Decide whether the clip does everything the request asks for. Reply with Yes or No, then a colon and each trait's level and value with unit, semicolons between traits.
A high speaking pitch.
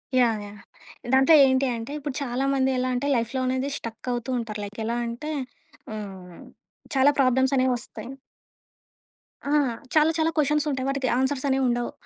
Yes: very high, 255 Hz